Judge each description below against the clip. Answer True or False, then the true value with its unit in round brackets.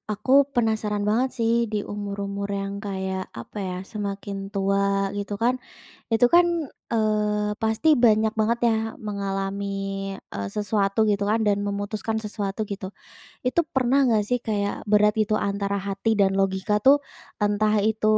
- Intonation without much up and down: True (1.8 semitones)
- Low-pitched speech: False (210 Hz)